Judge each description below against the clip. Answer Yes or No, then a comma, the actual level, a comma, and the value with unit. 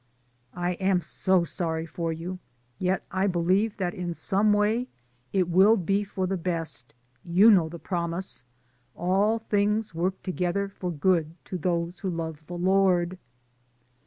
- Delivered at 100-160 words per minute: Yes, average, 150 wpm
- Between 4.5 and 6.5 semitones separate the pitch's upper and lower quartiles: No, narrow, 2.4 semitones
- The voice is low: No, medium, 180 Hz